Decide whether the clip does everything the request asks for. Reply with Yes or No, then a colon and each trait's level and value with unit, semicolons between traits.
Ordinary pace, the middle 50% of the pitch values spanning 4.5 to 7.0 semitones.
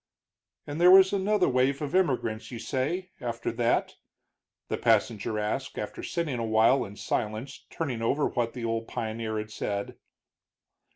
Yes: average, 155 wpm; average, 4.8 semitones